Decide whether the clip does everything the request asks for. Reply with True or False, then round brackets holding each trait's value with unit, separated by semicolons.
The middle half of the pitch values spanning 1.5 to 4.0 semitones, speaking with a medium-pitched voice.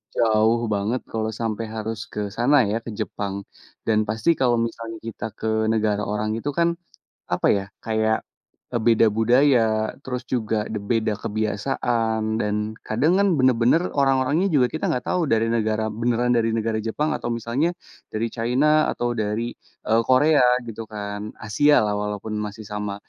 False (2.4 semitones; 115 Hz)